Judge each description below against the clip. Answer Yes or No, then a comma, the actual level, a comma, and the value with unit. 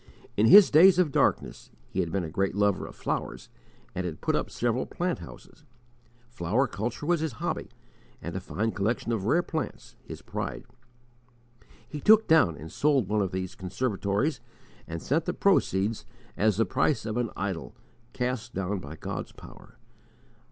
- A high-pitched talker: No, low, 110 Hz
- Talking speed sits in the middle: Yes, average, 170 wpm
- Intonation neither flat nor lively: No, wide, 7.4 semitones